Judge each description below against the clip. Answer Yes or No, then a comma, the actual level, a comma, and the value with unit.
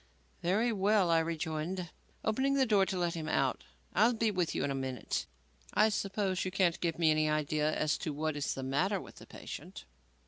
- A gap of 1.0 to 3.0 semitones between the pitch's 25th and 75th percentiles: No, average, 4.4 semitones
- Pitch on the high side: No, medium, 170 Hz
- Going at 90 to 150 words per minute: No, fast, 205 wpm